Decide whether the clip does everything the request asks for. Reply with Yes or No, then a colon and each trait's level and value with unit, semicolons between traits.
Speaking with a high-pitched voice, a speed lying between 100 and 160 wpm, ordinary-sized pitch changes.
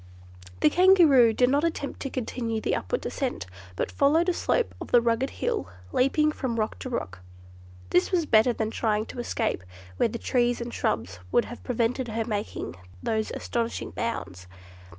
No: high, 235 Hz; average, 170 wpm; average, 3.5 semitones